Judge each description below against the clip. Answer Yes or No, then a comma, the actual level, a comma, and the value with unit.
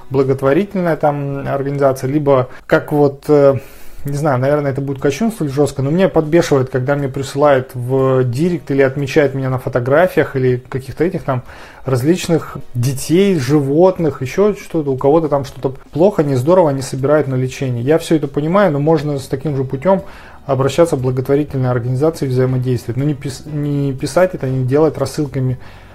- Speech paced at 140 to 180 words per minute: Yes, average, 155 wpm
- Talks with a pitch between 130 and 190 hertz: Yes, medium, 140 Hz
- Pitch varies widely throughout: No, narrow, 2.6 semitones